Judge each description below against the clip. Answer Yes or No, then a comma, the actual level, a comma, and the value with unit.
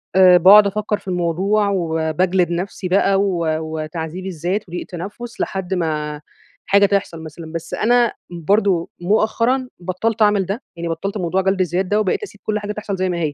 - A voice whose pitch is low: No, medium, 185 Hz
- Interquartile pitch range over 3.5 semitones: No, average, 3.2 semitones